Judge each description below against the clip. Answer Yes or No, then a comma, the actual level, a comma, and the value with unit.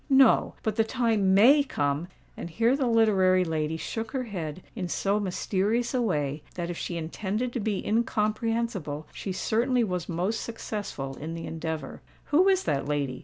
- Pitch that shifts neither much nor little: No, wide, 5.8 semitones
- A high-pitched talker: Yes, high, 200 Hz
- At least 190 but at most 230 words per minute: No, average, 170 wpm